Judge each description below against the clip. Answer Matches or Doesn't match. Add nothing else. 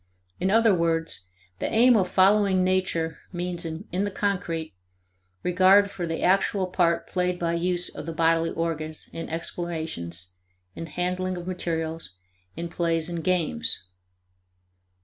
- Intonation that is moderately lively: Doesn't match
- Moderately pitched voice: Matches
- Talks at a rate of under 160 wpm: Matches